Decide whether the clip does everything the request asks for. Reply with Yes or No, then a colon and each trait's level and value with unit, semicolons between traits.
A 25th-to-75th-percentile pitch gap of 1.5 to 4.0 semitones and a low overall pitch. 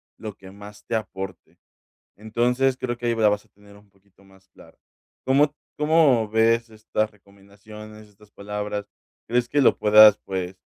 Yes: narrow, 2.6 semitones; low, 105 Hz